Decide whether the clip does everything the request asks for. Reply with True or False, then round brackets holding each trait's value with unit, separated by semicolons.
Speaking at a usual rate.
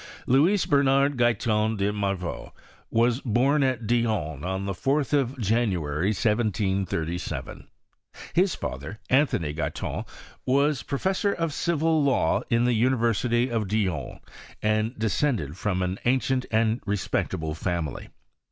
False (120 wpm)